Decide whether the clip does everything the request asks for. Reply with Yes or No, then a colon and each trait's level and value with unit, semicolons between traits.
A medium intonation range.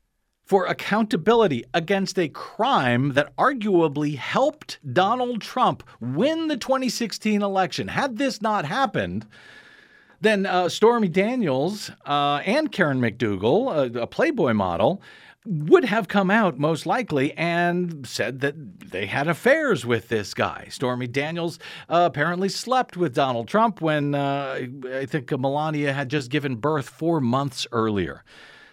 No: wide, 7.0 semitones